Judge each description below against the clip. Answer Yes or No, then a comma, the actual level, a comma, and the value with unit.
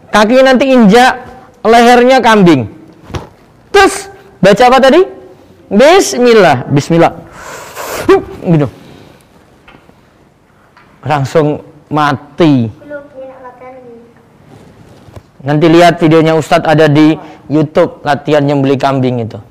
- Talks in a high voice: No, medium, 170 Hz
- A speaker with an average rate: No, slow, 80 wpm